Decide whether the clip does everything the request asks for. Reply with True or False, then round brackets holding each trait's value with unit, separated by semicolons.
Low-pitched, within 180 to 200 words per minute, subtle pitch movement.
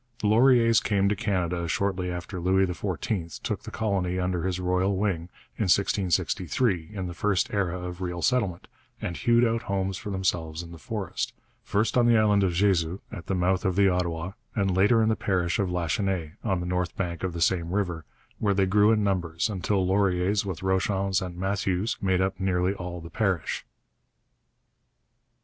True (95 Hz; 185 wpm; 2.2 semitones)